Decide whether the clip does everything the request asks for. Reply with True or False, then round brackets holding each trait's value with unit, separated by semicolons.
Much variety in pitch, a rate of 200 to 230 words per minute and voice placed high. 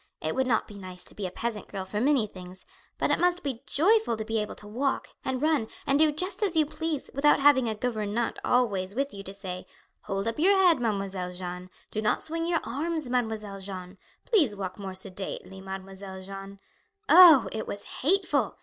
True (6.9 semitones; 205 wpm; 220 Hz)